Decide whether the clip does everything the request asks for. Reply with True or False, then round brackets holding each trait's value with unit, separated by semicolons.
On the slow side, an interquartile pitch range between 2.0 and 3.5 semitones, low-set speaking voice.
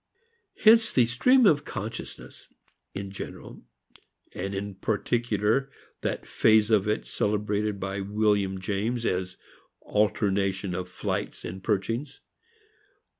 True (110 wpm; 2.9 semitones; 105 Hz)